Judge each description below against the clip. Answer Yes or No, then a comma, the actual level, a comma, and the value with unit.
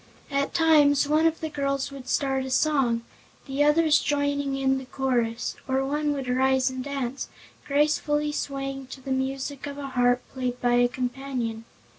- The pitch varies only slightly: Yes, narrow, 1.8 semitones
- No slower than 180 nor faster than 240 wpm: No, average, 170 wpm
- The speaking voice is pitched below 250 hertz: No, very high, 270 Hz